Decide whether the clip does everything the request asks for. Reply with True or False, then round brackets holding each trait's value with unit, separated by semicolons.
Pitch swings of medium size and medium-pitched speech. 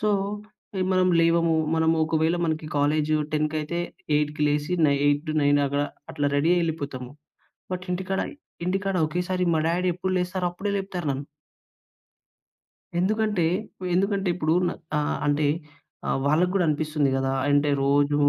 True (3.7 semitones; 160 Hz)